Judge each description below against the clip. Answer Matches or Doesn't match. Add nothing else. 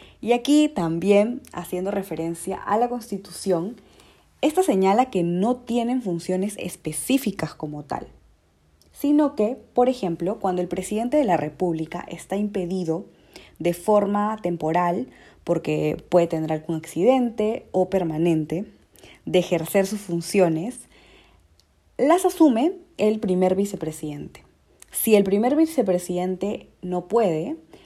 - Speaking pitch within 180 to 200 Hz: Matches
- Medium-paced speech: Doesn't match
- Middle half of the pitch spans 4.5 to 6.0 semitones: Matches